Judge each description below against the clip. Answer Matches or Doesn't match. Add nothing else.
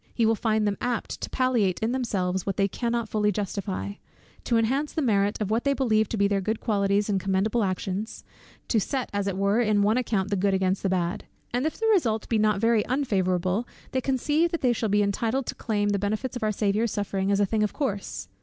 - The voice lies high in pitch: Matches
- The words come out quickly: Matches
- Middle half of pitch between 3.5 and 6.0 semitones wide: Doesn't match